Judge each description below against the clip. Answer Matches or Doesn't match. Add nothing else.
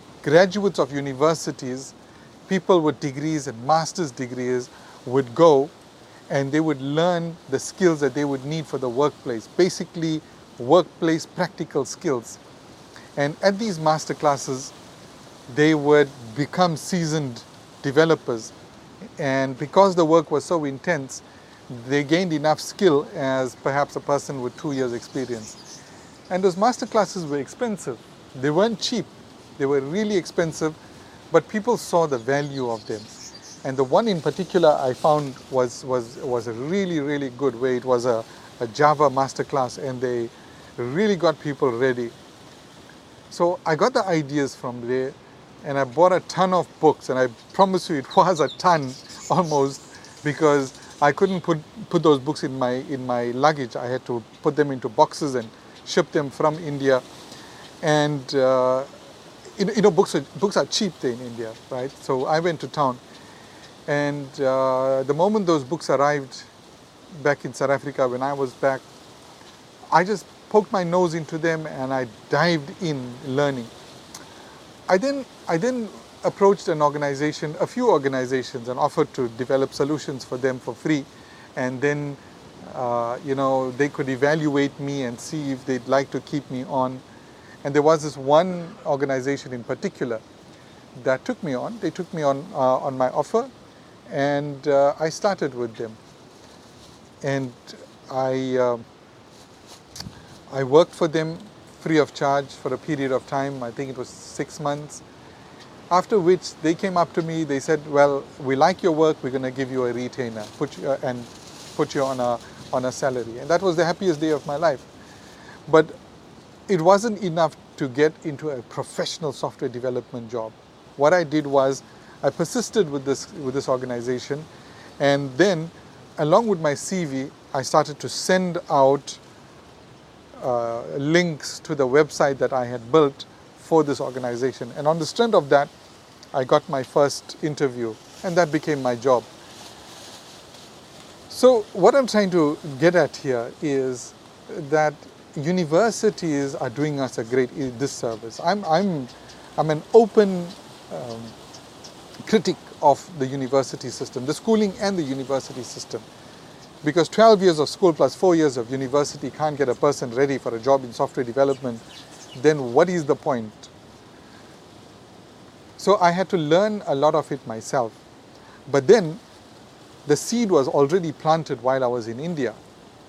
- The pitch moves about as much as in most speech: Matches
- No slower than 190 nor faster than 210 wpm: Doesn't match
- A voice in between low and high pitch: Matches